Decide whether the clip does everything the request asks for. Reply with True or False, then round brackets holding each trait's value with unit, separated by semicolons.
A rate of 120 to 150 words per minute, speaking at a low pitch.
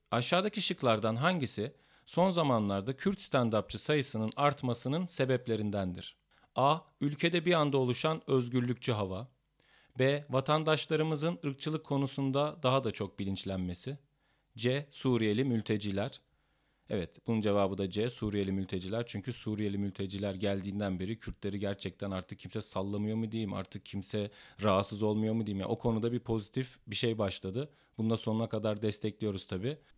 True (130 wpm; 115 Hz)